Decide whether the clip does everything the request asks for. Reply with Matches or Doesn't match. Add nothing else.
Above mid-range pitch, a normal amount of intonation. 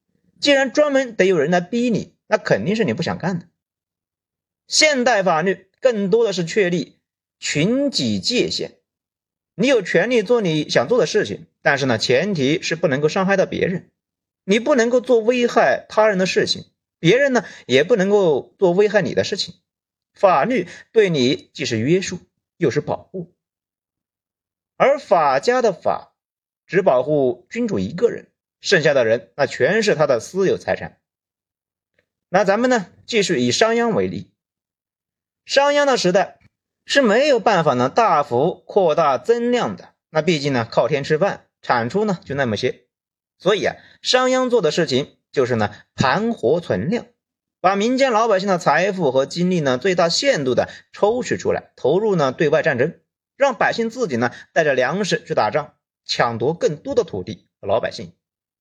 Doesn't match